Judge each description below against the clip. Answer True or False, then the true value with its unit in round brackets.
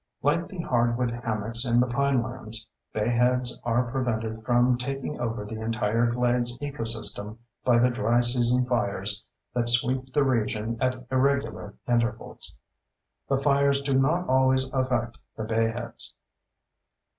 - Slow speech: True (130 wpm)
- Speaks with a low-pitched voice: True (120 Hz)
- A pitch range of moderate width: False (2.3 semitones)